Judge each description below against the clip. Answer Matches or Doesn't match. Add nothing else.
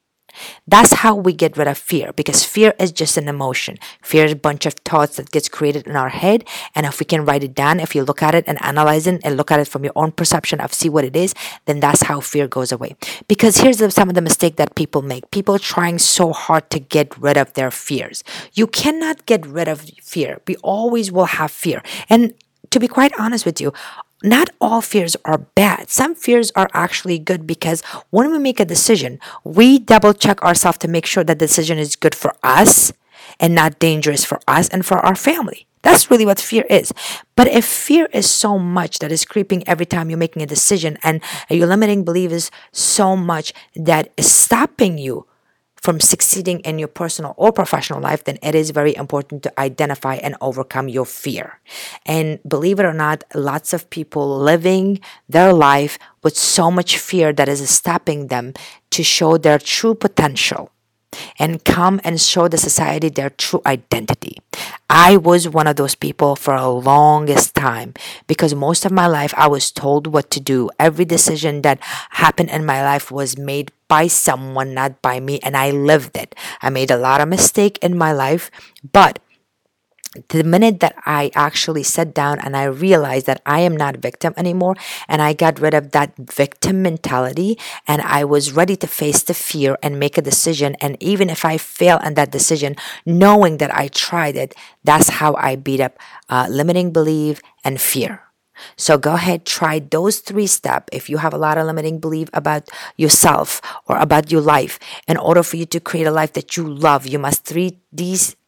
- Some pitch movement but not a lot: Matches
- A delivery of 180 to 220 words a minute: Matches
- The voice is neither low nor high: Matches